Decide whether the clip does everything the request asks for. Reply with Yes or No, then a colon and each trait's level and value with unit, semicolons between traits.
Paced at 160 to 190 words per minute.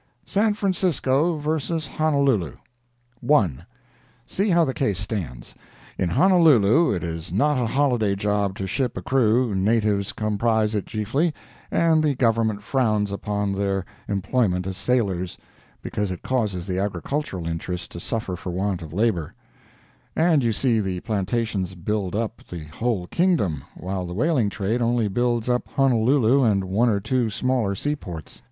No: average, 150 wpm